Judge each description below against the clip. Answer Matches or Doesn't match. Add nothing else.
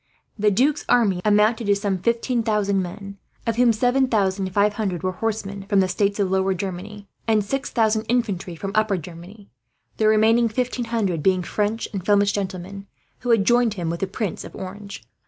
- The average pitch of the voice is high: Matches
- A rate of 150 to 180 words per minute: Doesn't match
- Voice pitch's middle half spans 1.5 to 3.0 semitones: Matches